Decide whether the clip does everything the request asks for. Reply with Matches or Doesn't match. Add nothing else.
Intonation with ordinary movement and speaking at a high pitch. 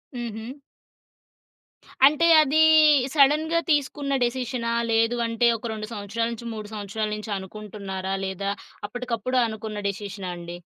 Matches